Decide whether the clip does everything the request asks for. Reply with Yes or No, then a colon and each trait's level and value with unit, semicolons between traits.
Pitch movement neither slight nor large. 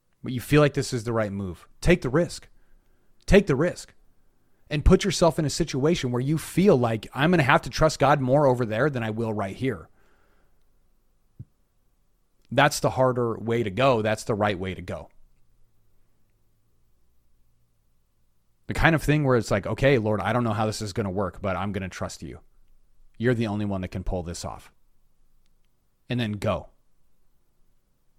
No: wide, 6.2 semitones